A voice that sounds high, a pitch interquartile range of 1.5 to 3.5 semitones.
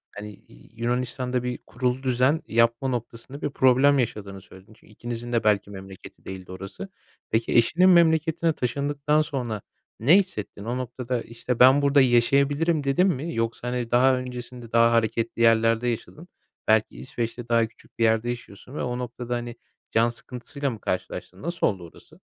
No: low, 120 Hz; average, 3.1 semitones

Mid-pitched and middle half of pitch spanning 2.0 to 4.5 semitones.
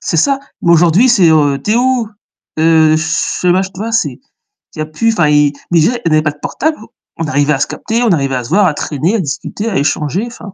No: medium, 165 Hz; wide, 6.1 semitones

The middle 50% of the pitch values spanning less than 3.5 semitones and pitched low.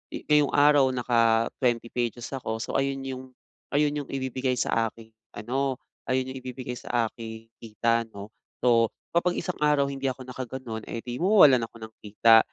Yes: average, 2.9 semitones; low, 125 Hz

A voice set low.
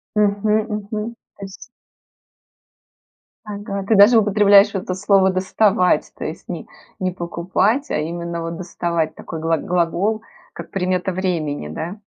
No: high, 190 Hz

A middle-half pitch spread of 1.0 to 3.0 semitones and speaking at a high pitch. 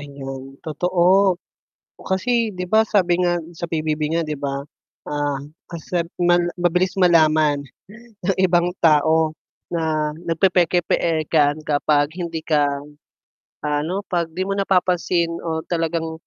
No: average, 2.7 semitones; medium, 165 Hz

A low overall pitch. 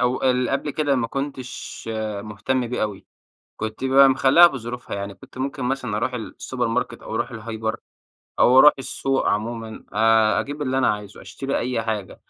Yes: low, 125 Hz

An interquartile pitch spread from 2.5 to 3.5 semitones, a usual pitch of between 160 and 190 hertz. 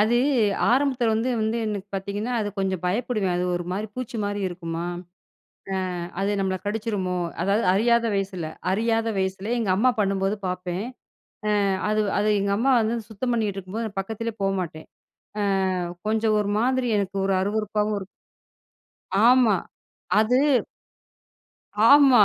No: average, 2.9 semitones; high, 210 Hz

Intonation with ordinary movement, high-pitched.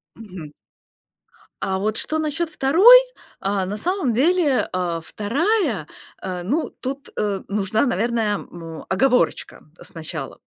No: wide, 7.9 semitones; high, 225 Hz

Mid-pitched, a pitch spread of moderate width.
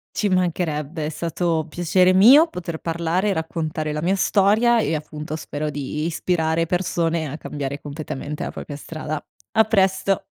Yes: medium, 165 Hz; average, 3.3 semitones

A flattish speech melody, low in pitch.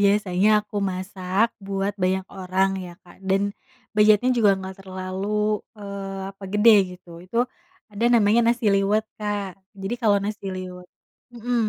No: narrow, 2.0 semitones; high, 200 Hz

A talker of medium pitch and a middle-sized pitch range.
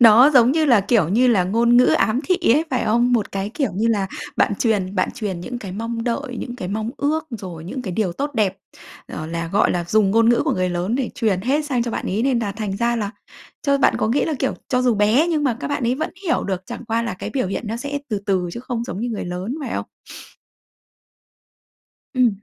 No: high, 230 Hz; average, 4.3 semitones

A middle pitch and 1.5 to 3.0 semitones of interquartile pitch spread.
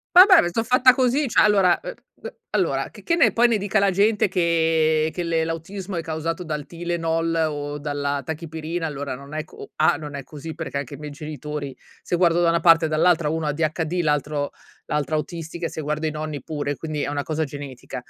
Yes: medium, 160 Hz; narrow, 2.6 semitones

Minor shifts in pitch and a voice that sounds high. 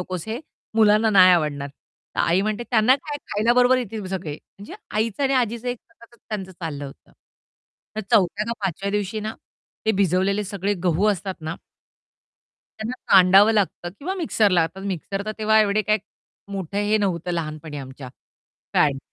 No: average, 3.4 semitones; high, 200 Hz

